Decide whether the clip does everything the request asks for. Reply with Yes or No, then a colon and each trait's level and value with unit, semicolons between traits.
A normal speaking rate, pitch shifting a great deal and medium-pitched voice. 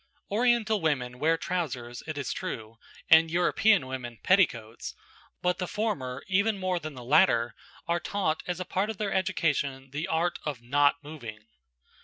Yes: average, 160 wpm; wide, 6.4 semitones; medium, 160 Hz